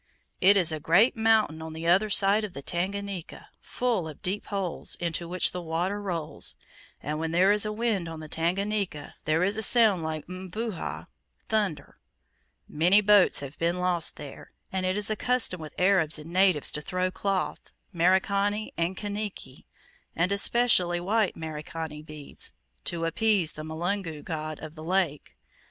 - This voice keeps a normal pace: Yes, average, 165 wpm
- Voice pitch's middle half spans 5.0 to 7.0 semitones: No, average, 3.9 semitones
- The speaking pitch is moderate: Yes, medium, 180 Hz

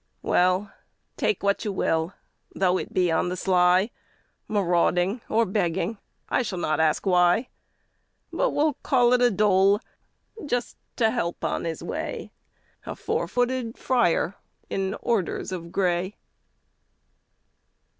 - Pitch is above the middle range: Yes, high, 195 Hz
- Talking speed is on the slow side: Yes, slow, 130 wpm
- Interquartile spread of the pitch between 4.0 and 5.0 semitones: Yes, average, 4.4 semitones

